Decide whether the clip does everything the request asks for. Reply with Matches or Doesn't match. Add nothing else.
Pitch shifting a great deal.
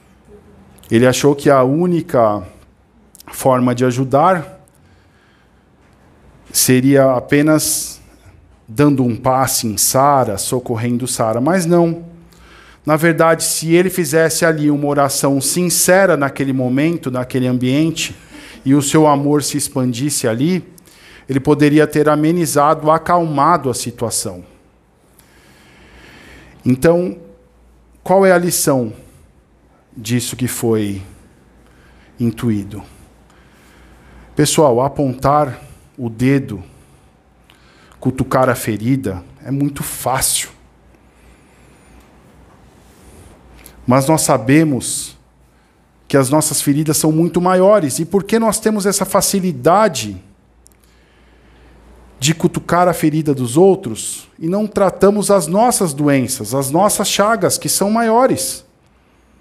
Matches